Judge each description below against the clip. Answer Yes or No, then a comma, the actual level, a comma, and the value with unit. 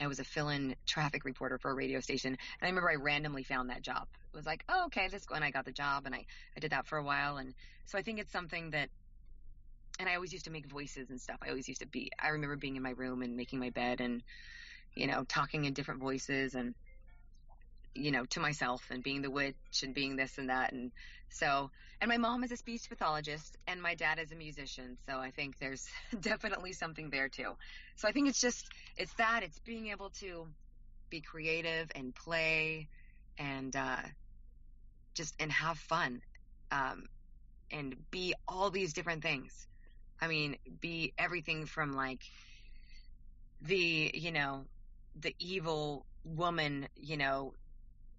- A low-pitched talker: No, medium, 145 Hz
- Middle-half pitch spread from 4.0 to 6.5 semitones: Yes, average, 4.4 semitones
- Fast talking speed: No, average, 195 wpm